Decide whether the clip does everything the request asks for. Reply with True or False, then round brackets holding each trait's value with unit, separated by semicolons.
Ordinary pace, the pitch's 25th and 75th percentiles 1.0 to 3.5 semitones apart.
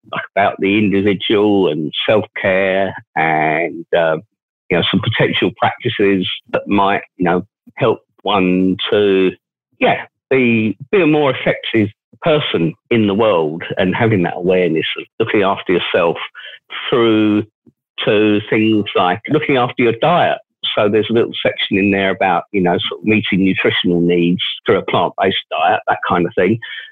True (160 wpm; 2.6 semitones)